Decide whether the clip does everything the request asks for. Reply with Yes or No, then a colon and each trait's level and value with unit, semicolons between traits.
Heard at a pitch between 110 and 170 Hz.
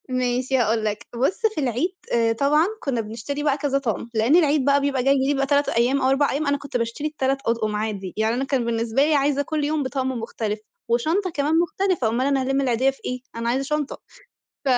No: very high, 270 Hz